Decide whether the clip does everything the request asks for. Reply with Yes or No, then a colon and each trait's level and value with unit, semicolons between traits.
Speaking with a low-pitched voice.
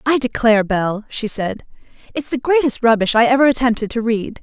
No: high, 235 Hz